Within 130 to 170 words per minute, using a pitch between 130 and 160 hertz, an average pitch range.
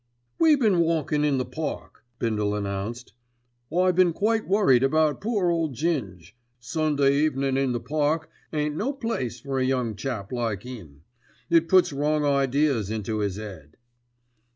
No: average, 155 wpm; medium, 140 Hz; wide, 5.7 semitones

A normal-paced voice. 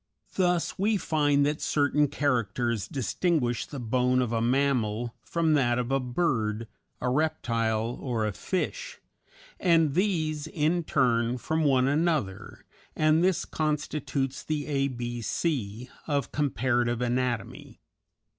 No: slow, 125 wpm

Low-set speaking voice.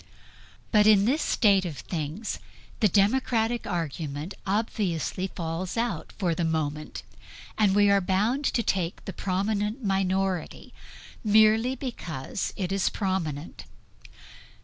No: high, 195 Hz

